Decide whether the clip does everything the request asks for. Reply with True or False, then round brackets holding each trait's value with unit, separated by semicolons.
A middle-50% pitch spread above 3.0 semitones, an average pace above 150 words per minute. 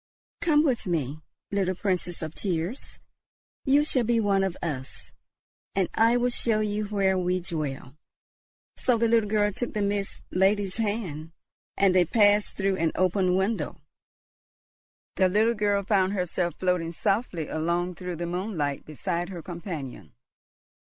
False (3.4 semitones; 145 wpm)